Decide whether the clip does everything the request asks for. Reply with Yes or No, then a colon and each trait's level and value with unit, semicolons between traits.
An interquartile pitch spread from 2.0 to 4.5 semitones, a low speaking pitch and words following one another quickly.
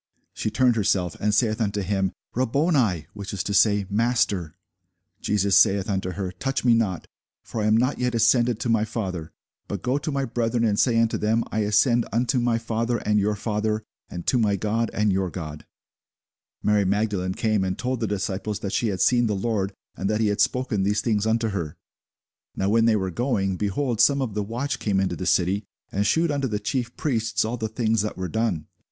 Yes: average, 2.9 semitones; low, 110 Hz; fast, 210 wpm